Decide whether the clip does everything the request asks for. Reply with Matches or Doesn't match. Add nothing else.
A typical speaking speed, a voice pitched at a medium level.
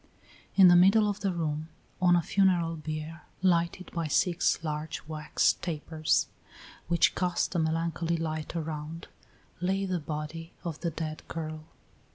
Matches